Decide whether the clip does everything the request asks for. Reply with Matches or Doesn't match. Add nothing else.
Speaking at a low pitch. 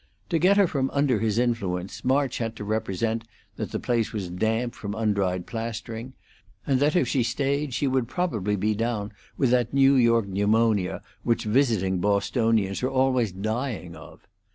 Matches